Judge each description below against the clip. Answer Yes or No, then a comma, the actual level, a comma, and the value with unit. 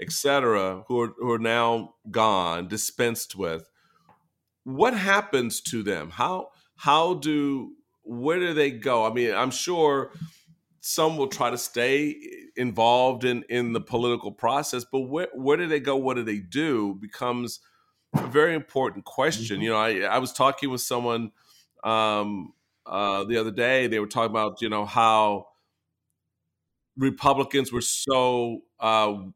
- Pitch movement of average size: Yes, average, 4.2 semitones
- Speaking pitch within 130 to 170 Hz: No, low, 120 Hz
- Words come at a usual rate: Yes, average, 150 wpm